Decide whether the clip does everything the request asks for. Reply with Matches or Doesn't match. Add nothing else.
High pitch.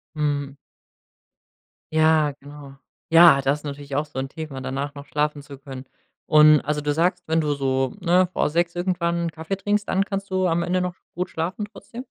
Doesn't match